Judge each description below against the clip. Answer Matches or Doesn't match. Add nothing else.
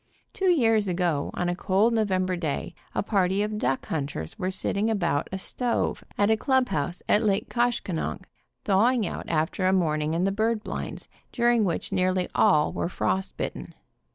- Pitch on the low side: Doesn't match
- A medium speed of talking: Matches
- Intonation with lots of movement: Doesn't match